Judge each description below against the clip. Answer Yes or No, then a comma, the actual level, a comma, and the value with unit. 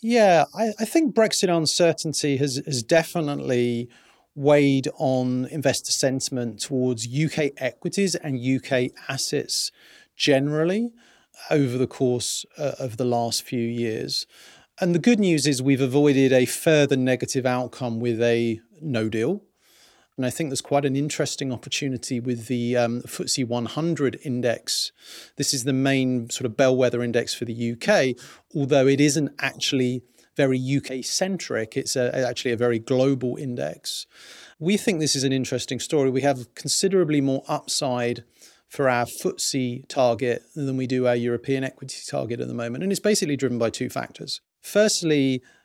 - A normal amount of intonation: Yes, average, 3.3 semitones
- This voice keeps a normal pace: Yes, average, 155 wpm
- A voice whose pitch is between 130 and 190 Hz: Yes, low, 135 Hz